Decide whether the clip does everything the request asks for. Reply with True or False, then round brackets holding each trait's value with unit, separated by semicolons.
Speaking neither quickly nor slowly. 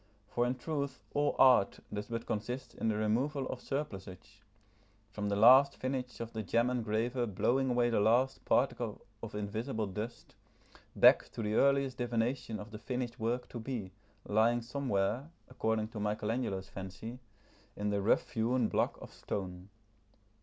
True (155 wpm)